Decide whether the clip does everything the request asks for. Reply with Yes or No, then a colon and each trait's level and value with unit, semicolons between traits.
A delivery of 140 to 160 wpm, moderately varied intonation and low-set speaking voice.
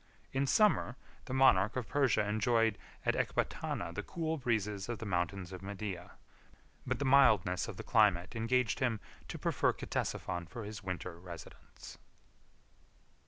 Yes: average, 145 wpm; average, 4.9 semitones; low, 105 Hz